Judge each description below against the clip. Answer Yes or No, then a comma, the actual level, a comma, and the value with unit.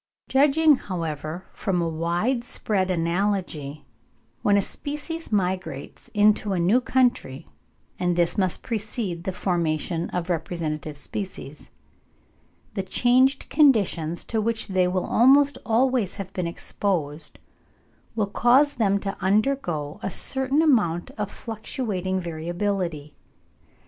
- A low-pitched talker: No, high, 190 Hz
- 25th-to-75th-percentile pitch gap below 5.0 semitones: No, wide, 5.5 semitones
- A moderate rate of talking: No, slow, 120 wpm